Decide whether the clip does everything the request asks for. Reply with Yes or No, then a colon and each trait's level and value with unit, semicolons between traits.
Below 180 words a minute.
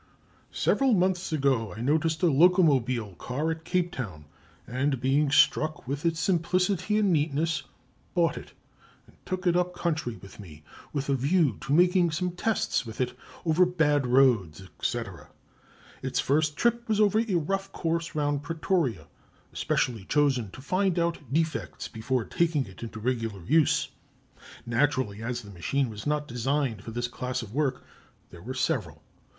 Yes: average, 160 wpm